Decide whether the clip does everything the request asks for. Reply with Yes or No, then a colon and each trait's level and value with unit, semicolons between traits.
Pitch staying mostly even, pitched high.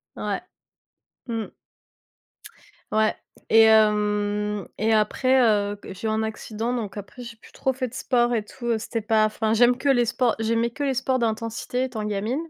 Yes: narrow, 2.3 semitones; high, 225 Hz